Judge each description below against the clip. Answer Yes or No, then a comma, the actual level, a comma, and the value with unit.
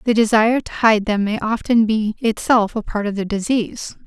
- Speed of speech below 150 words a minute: No, fast, 205 wpm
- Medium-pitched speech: No, high, 220 Hz